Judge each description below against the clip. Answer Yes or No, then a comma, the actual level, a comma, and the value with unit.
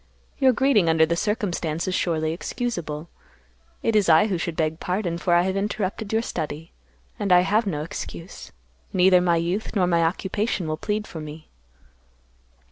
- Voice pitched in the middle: Yes, medium, 180 Hz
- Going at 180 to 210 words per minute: No, average, 170 wpm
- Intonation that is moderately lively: Yes, average, 4.1 semitones